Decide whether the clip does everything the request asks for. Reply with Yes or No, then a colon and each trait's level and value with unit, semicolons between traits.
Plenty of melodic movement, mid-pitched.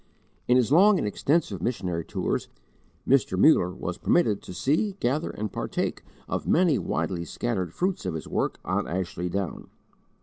No: wide, 9.0 semitones; low, 110 Hz